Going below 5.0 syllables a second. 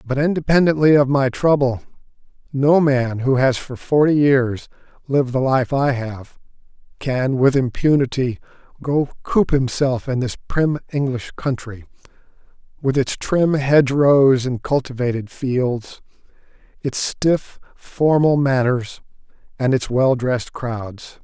Yes: 4.0 syllables/s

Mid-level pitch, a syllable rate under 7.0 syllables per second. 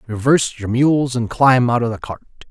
No: low, 125 Hz; 5.1 syllables/s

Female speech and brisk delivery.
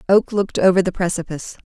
No: female; average, 180 wpm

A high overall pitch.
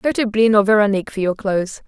Yes: high, 210 Hz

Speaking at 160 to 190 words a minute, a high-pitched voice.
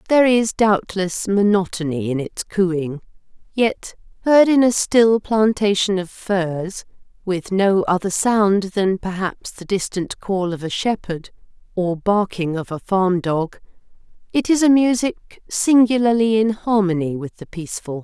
No: average, 145 wpm; high, 195 Hz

